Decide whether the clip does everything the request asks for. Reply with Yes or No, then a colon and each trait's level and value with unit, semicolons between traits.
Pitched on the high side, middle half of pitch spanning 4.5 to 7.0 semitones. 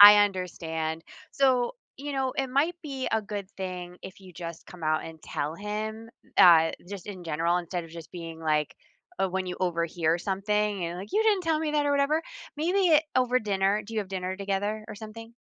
Yes: high, 195 Hz; average, 5.0 semitones